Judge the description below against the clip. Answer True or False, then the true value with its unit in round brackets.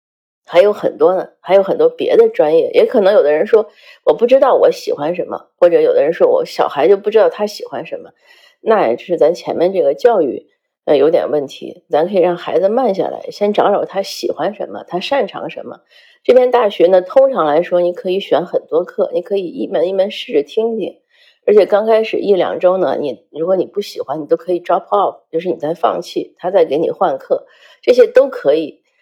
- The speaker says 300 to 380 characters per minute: True (320 characters per minute)